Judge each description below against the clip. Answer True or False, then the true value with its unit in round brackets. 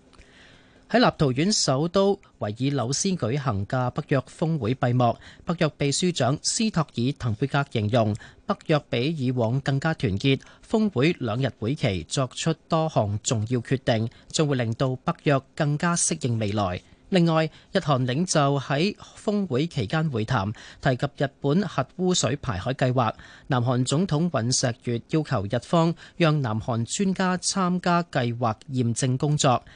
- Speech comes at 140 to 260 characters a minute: True (230 characters per minute)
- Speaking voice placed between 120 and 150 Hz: True (140 Hz)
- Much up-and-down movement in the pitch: False (4.7 semitones)